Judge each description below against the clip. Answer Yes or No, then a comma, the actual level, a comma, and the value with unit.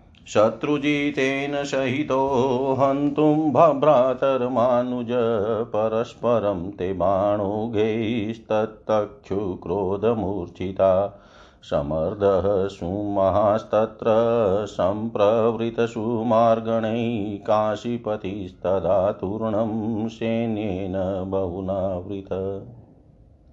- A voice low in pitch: Yes, low, 110 Hz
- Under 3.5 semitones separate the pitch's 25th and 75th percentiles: Yes, average, 3.1 semitones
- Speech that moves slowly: Yes, slow, 35 wpm